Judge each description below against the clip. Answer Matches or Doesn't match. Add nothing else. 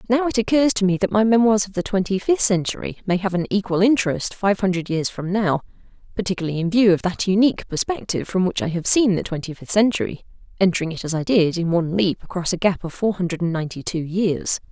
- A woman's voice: Matches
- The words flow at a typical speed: Doesn't match